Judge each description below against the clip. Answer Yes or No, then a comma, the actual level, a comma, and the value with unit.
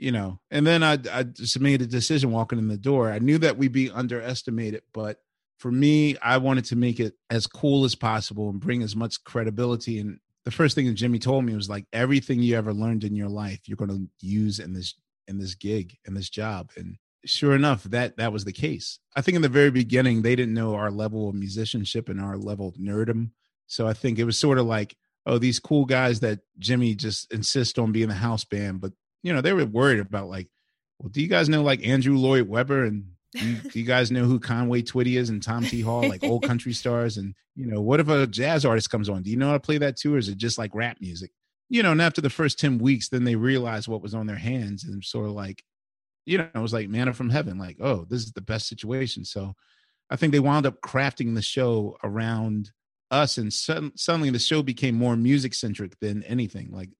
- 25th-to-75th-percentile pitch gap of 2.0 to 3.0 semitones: No, average, 3.8 semitones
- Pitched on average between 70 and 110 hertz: No, low, 120 Hz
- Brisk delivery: Yes, fast, 240 wpm